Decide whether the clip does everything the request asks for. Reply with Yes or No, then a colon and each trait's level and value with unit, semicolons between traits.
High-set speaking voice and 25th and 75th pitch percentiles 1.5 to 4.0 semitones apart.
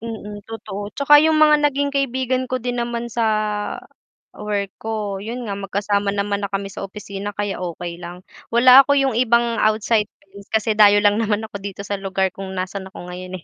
Yes: high, 210 Hz; average, 3.3 semitones